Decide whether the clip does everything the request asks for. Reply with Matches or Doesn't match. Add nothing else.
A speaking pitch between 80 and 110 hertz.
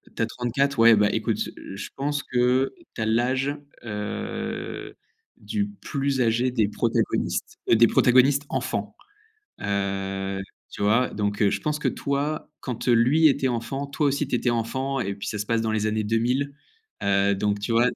Doesn't match